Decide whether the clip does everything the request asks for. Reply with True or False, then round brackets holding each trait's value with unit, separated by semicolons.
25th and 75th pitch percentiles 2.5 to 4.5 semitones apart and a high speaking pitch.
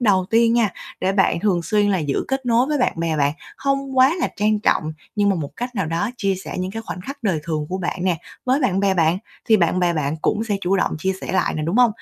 False (5.0 semitones; 195 Hz)